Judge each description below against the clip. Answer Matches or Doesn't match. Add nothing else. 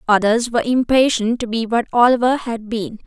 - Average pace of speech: Matches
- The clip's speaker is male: Doesn't match